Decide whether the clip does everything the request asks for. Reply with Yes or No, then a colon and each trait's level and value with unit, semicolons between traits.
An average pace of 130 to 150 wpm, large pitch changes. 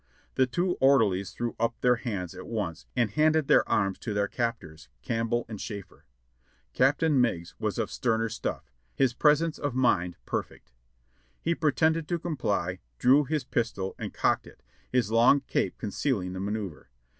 No: average, 165 wpm; wide, 5.7 semitones